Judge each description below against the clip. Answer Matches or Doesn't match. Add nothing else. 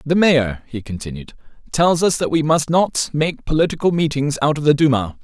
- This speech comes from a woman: Doesn't match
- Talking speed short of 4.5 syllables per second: Doesn't match